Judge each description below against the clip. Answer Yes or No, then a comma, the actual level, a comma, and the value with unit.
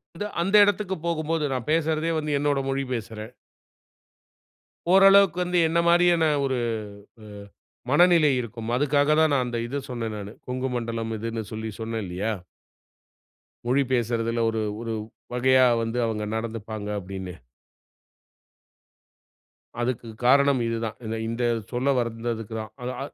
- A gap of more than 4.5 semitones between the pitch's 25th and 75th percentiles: Yes, average, 4.9 semitones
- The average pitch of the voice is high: No, low, 125 Hz